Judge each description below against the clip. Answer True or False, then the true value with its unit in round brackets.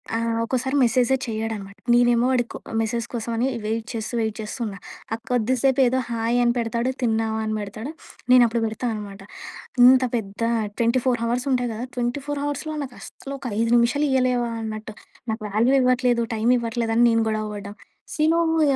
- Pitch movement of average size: False (2.2 semitones)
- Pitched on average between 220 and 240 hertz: True (235 Hz)